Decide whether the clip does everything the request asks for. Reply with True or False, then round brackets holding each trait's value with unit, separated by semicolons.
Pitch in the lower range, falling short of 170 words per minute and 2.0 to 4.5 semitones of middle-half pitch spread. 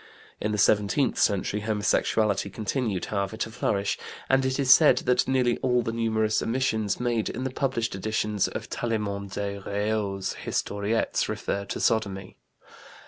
True (110 Hz; 145 wpm; 3.0 semitones)